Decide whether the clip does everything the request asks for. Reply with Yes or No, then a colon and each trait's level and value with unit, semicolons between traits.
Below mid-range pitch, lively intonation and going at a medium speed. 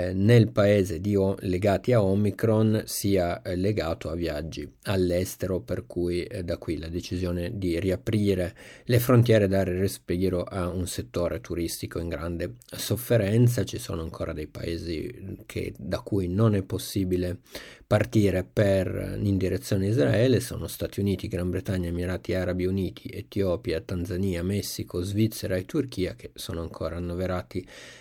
No: very low, 95 Hz; average, 2.8 semitones; average, 140 wpm